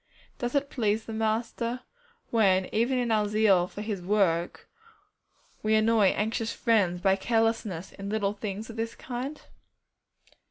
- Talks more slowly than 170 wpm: Yes, average, 145 wpm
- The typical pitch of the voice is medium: No, high, 220 Hz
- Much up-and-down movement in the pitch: No, narrow, 2.5 semitones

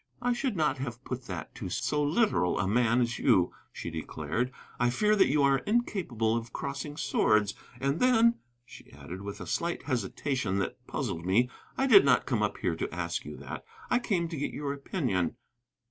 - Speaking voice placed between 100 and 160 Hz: Yes, low, 135 Hz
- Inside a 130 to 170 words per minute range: No, average, 190 wpm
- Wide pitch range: Yes, wide, 7.4 semitones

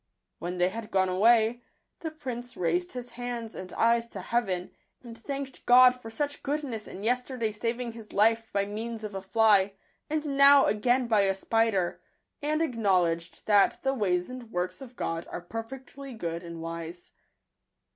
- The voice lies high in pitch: Yes, high, 225 Hz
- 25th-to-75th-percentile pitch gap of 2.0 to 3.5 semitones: No, average, 4.7 semitones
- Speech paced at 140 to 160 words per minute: No, average, 175 wpm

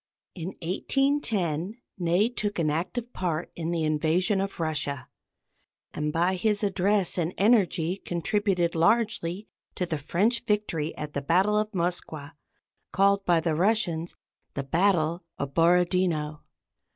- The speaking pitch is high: No, medium, 175 Hz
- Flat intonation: No, average, 4.0 semitones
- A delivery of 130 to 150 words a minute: Yes, slow, 135 wpm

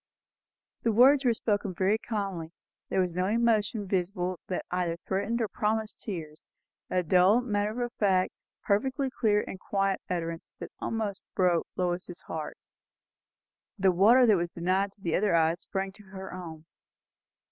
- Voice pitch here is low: No, high, 195 Hz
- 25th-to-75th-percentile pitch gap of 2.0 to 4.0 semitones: Yes, average, 3.2 semitones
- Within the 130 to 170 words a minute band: Yes, average, 155 wpm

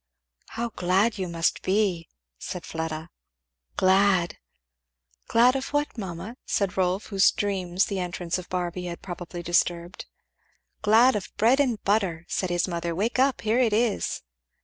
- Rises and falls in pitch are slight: No, average, 3.9 semitones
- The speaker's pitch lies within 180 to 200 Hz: Yes, medium, 185 Hz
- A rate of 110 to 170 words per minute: Yes, average, 150 wpm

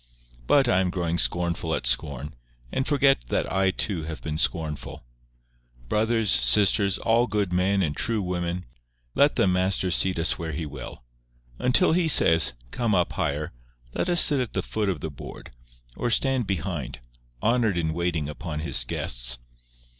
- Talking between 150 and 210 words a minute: Yes, average, 165 wpm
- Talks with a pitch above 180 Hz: No, very low, 90 Hz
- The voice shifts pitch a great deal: Yes, wide, 5.7 semitones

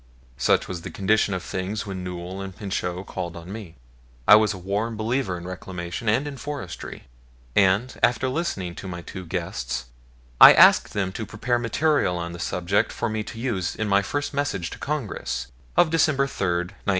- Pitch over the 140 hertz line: No, low, 100 Hz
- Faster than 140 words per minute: Yes, average, 185 wpm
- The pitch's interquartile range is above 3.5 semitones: Yes, average, 4.7 semitones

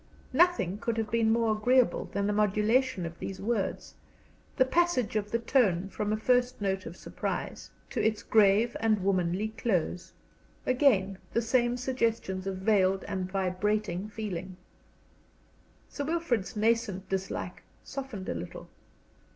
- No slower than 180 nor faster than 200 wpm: No, average, 140 wpm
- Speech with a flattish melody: No, average, 3.7 semitones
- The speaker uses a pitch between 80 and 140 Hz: No, high, 215 Hz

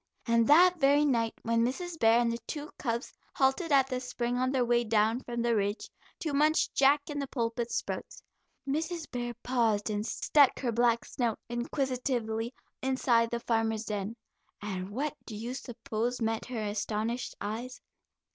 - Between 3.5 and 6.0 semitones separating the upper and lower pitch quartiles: No, average, 3.0 semitones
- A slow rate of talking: No, average, 165 wpm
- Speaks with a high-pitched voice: Yes, high, 240 Hz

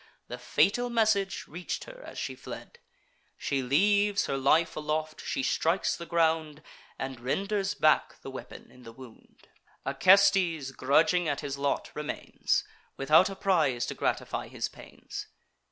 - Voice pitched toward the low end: No, medium, 160 Hz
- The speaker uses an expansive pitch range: Yes, wide, 6.1 semitones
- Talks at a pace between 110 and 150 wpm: Yes, average, 145 wpm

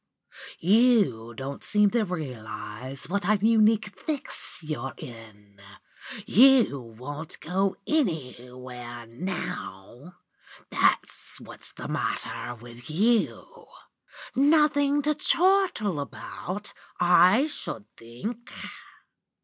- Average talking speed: No, slow, 90 wpm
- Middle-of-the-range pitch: Yes, medium, 175 Hz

